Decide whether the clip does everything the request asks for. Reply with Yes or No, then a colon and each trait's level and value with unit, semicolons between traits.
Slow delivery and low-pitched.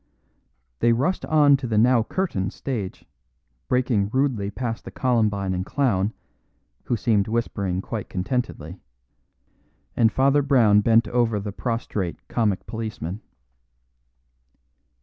Yes: slow, 115 wpm; low, 115 Hz